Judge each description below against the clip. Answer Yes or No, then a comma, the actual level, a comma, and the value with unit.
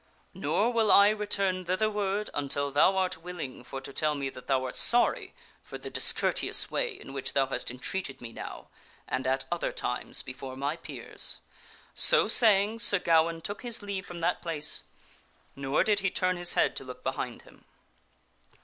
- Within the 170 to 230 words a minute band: Yes, average, 175 wpm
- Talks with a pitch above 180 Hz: No, medium, 175 Hz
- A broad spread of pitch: Yes, wide, 6.6 semitones